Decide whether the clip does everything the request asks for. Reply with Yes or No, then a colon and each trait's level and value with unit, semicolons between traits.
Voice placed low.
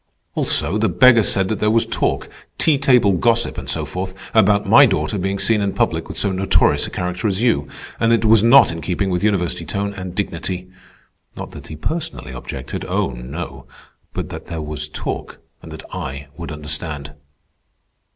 Yes: very low, 95 Hz